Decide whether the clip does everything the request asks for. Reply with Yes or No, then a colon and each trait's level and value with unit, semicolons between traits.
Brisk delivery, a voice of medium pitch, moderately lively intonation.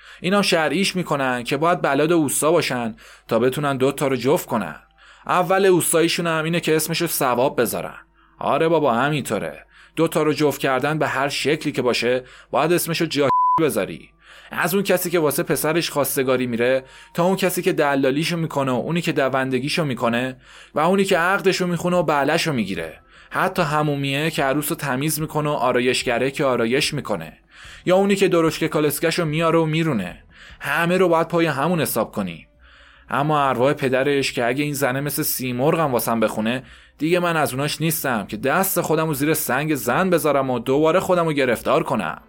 Yes: fast, 175 wpm; medium, 150 Hz; average, 4.1 semitones